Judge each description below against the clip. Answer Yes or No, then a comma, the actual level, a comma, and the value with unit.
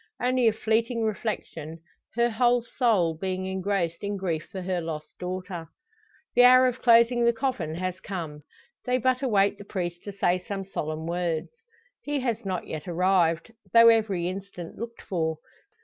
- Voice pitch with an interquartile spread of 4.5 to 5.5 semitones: Yes, average, 5.0 semitones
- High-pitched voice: Yes, high, 195 Hz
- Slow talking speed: No, average, 165 wpm